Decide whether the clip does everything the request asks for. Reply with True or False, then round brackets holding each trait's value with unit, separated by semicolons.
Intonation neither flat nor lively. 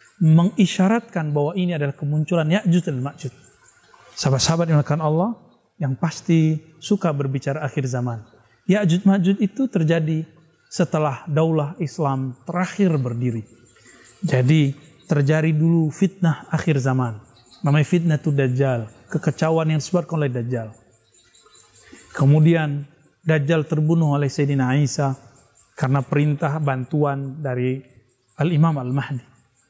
True (3.7 semitones)